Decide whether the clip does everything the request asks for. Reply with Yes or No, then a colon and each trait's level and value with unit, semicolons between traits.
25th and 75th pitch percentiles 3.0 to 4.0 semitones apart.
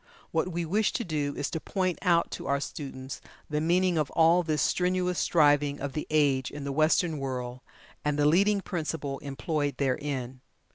Yes: average, 3.6 semitones